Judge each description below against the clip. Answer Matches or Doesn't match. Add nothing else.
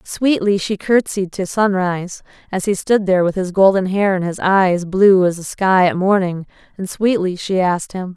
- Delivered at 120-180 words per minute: Doesn't match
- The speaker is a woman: Matches